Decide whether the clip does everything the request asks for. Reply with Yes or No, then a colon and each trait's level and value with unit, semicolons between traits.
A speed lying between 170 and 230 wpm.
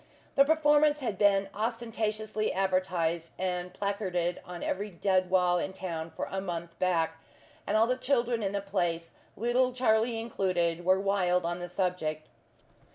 No: average, 155 wpm